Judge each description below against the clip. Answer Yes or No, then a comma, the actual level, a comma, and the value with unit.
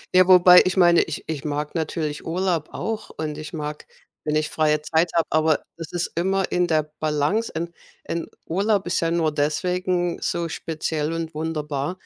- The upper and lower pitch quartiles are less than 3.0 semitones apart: Yes, narrow, 2.6 semitones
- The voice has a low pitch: No, medium, 165 Hz